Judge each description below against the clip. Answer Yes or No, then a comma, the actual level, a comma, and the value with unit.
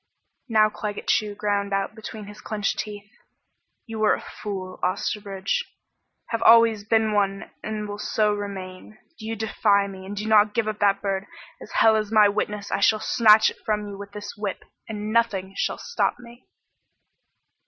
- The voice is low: No, high, 210 Hz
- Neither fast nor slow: Yes, average, 175 wpm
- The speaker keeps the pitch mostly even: Yes, narrow, 1.4 semitones